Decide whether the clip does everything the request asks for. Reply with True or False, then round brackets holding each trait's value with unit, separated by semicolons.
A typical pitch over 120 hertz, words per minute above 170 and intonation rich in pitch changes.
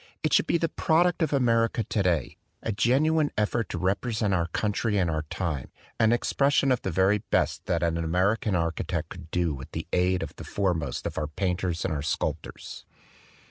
False (95 Hz; 180 wpm; 5.7 semitones)